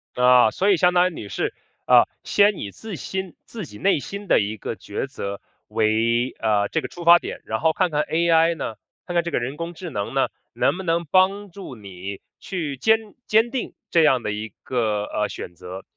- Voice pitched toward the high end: No, medium, 155 Hz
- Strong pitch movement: Yes, wide, 8.8 semitones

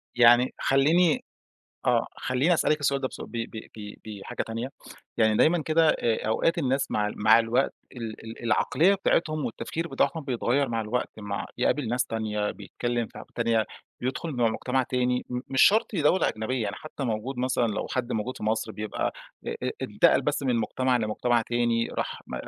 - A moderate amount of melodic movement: Yes, average, 3.5 semitones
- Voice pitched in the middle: No, low, 125 Hz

